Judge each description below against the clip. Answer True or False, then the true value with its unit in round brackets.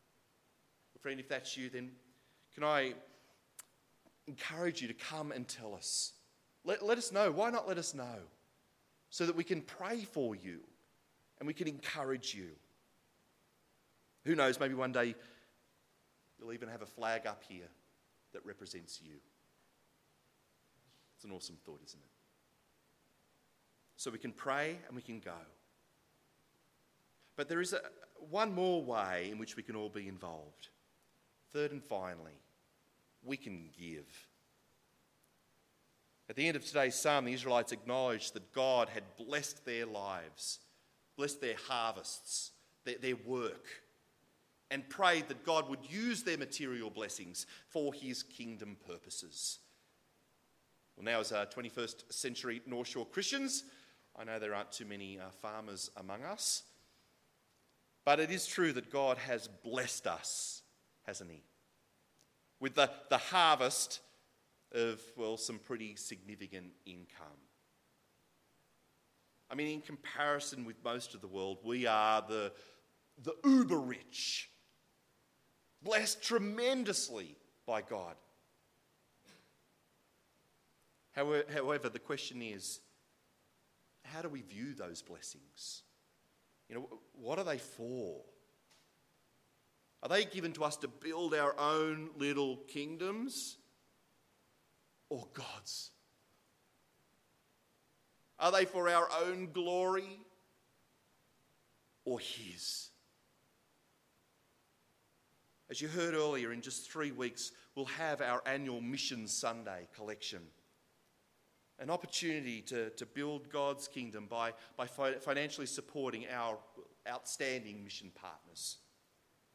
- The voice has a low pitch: True (130 Hz)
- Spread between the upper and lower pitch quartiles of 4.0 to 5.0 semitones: False (5.6 semitones)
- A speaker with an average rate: False (125 wpm)